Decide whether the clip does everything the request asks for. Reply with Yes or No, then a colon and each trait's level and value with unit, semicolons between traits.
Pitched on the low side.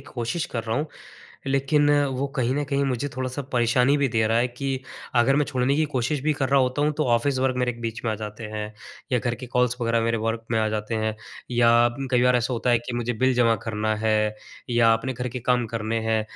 Yes: low, 120 Hz